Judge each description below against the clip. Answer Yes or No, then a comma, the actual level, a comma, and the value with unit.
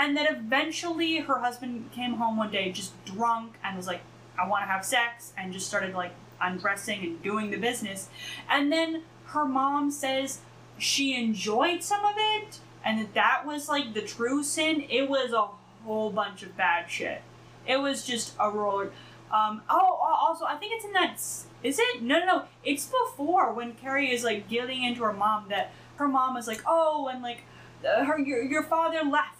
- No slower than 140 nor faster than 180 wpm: No, average, 195 wpm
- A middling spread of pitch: No, wide, 5.7 semitones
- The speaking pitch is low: No, high, 245 Hz